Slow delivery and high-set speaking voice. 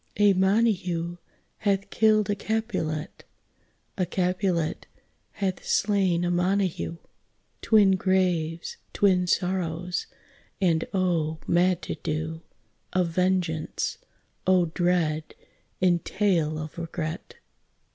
No: slow, 95 wpm; medium, 180 Hz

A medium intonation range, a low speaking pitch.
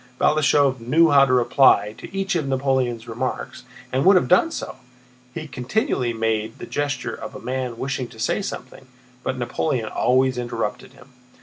Yes: average, 3.1 semitones; low, 130 Hz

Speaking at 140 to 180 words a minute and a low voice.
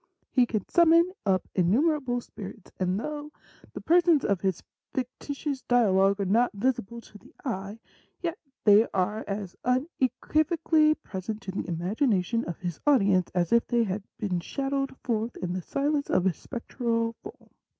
No: average, 160 wpm; high, 230 Hz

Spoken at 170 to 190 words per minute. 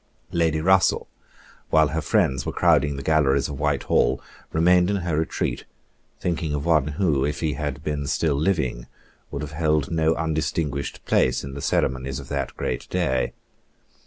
No: average, 160 wpm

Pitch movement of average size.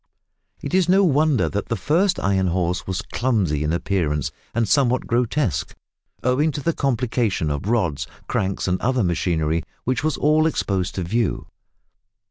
No: wide, 7.3 semitones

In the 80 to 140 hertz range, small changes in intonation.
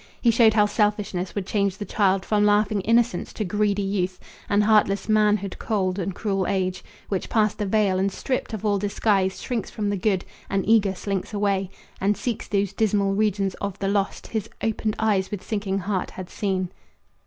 No: high, 200 Hz; narrow, 1.7 semitones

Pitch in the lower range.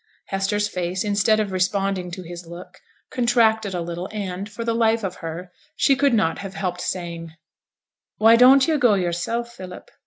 No: high, 195 Hz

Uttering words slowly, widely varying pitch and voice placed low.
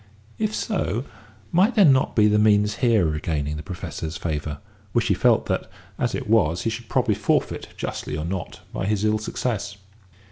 No: average, 185 wpm; wide, 5.8 semitones; low, 105 Hz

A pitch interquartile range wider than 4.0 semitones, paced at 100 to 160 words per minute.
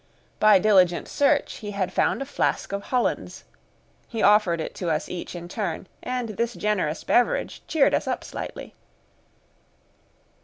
Yes: average, 4.6 semitones; average, 150 wpm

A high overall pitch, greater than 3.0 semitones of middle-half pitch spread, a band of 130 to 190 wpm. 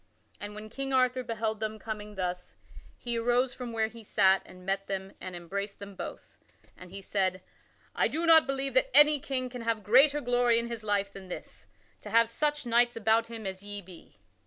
No: high, 225 Hz; average, 3.9 semitones; fast, 205 wpm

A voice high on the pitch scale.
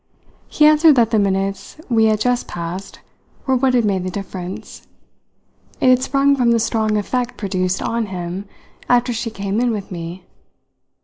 Yes: high, 220 Hz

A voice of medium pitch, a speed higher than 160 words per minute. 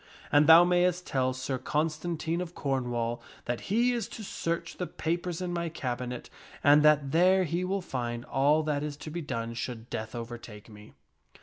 Yes: medium, 150 Hz; average, 180 wpm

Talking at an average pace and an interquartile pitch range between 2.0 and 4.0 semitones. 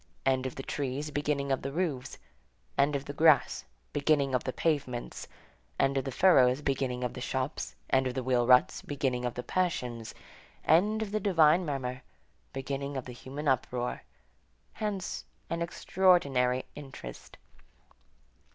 Yes: average, 150 wpm; average, 3.1 semitones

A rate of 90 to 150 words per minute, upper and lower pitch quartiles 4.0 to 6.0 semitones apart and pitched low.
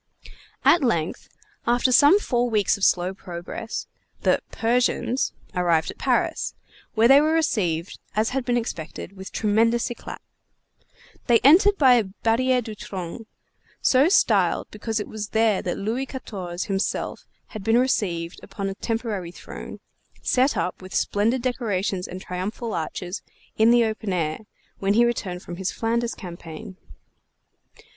No: average, 145 wpm; average, 4.5 semitones; high, 220 Hz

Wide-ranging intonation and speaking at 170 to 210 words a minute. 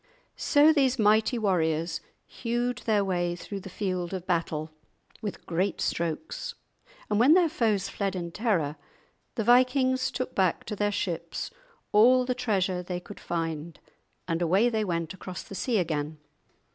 No: wide, 5.8 semitones; average, 155 wpm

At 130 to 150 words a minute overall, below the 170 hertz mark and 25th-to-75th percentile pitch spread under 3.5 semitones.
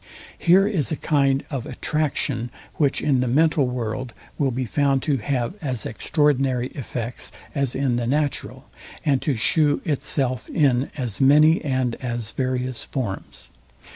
Yes: average, 145 wpm; low, 135 Hz; average, 2.9 semitones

